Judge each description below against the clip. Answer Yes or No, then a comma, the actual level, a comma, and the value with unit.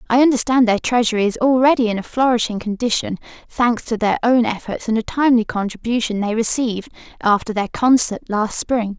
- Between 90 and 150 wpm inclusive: No, average, 175 wpm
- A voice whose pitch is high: Yes, high, 230 Hz